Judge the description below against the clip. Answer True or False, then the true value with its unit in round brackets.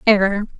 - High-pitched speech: True (205 Hz)